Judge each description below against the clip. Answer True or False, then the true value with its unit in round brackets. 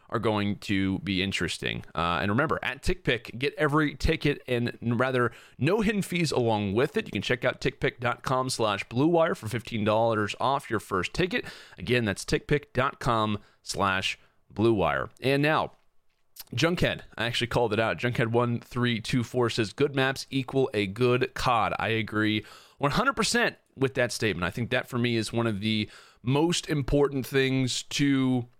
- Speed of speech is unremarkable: True (160 wpm)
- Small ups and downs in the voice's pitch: False (3.9 semitones)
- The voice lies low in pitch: True (125 Hz)